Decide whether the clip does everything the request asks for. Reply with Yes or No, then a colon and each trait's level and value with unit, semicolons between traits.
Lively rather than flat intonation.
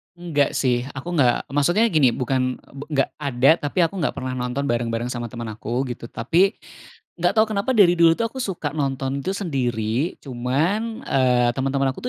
Yes: wide, 5.8 semitones